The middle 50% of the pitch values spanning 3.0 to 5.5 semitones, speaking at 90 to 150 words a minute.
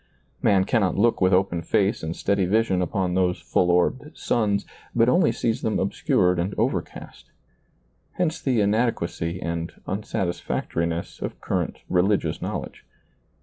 Yes: average, 3.8 semitones; average, 140 wpm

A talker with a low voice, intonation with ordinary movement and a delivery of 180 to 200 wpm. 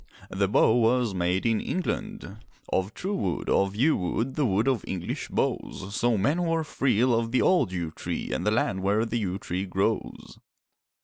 Yes: low, 110 Hz; average, 5.0 semitones; average, 190 wpm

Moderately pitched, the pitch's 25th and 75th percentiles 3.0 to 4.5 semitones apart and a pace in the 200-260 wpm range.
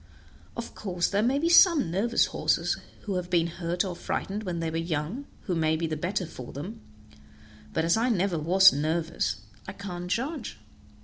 No: medium, 180 Hz; average, 4.2 semitones; average, 185 wpm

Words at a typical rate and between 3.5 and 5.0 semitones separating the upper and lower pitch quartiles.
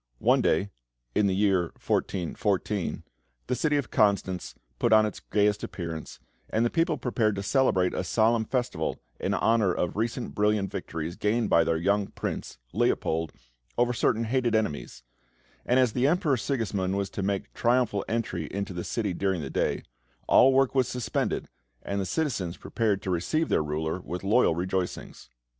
Yes: average, 170 wpm; average, 4.5 semitones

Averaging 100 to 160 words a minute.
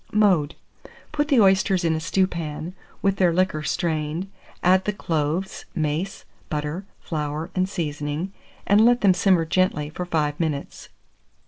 Yes: average, 140 wpm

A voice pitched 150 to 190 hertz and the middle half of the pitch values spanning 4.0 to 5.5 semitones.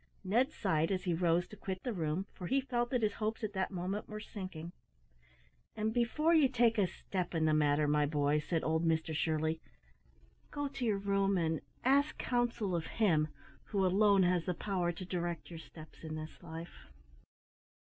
Yes: medium, 185 Hz; average, 4.9 semitones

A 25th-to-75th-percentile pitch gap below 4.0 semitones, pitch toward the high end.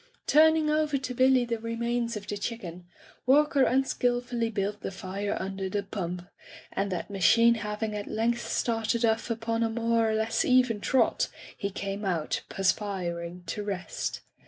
Yes: average, 3.3 semitones; high, 225 Hz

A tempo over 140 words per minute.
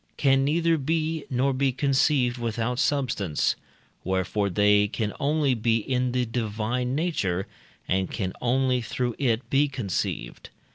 No: slow, 135 wpm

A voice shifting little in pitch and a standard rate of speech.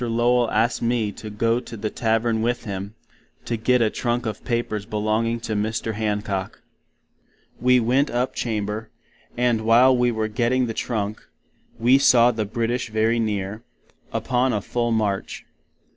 Yes: narrow, 2.0 semitones; average, 155 wpm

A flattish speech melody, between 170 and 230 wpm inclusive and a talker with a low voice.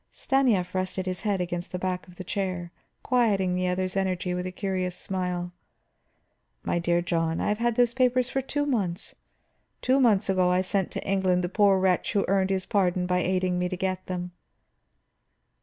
No: narrow, 1.8 semitones; average, 190 wpm; medium, 185 Hz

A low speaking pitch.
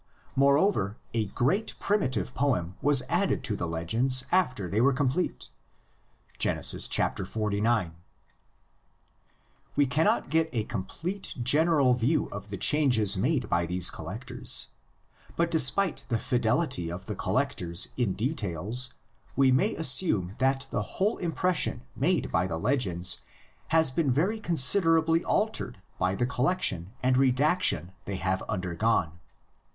Yes: low, 125 Hz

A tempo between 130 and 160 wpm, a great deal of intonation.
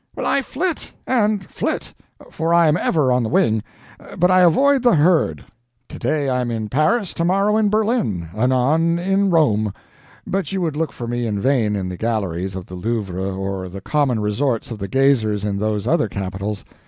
No: average, 185 wpm; wide, 8.8 semitones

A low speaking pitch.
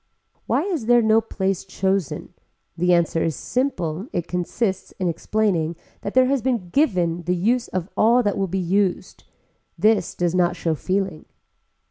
No: high, 190 Hz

